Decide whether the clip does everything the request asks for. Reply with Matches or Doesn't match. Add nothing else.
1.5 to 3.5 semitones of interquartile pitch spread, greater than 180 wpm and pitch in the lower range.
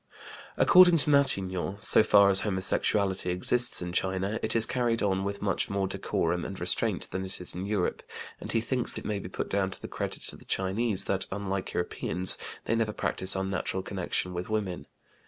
Matches